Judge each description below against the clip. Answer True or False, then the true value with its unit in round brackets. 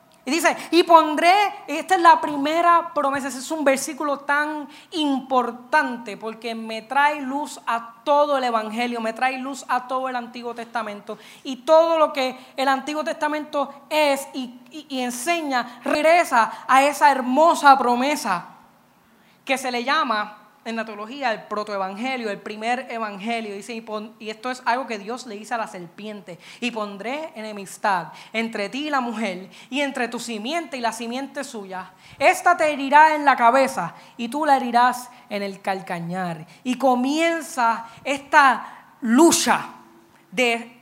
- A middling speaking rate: True (160 wpm)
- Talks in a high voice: True (255 Hz)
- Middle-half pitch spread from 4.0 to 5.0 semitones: True (4.6 semitones)